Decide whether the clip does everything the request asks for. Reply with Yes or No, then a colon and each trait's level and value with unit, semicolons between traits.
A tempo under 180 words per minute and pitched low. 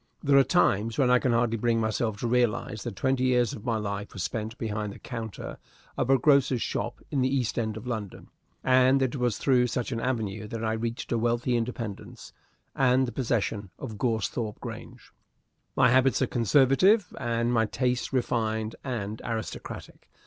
No: average, 185 wpm; low, 120 Hz